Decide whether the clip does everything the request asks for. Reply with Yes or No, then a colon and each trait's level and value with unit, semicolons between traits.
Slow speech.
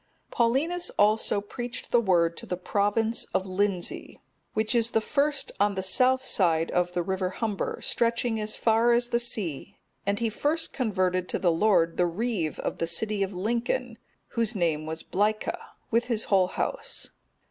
No: average, 175 wpm